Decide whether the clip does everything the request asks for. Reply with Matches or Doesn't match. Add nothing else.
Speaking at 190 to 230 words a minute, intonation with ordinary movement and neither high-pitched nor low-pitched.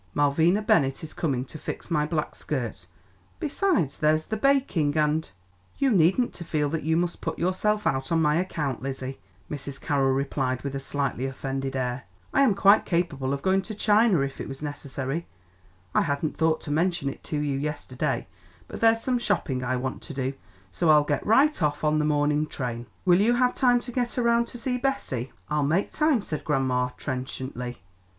Doesn't match